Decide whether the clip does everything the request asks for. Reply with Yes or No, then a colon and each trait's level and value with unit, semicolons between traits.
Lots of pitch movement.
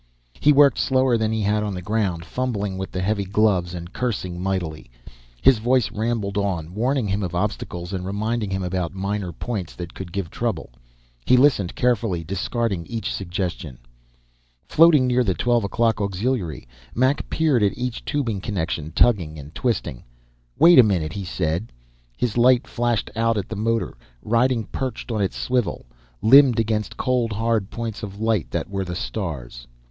No: average, 4.4 semitones